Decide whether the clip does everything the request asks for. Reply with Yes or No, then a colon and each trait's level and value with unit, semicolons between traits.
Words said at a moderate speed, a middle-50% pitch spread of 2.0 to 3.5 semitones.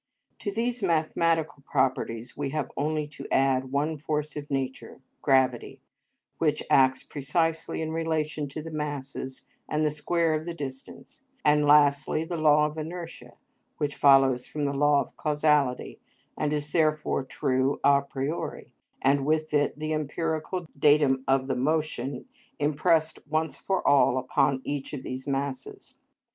Yes: average, 150 wpm; narrow, 2.4 semitones